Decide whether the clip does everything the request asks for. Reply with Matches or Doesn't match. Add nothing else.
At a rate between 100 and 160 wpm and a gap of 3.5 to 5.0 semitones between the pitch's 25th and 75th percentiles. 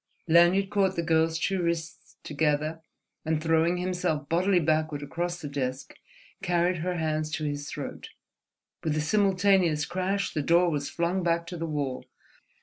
Doesn't match